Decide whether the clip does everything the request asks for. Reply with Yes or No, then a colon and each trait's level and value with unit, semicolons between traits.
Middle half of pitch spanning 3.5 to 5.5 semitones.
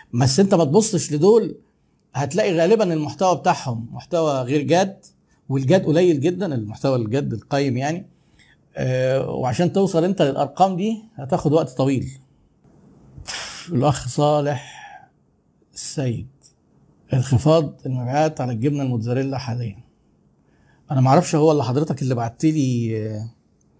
Yes: average, 4.7 semitones